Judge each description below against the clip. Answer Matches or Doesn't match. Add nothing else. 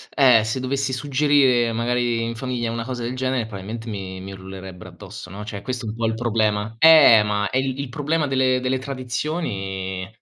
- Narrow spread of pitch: Doesn't match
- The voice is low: Matches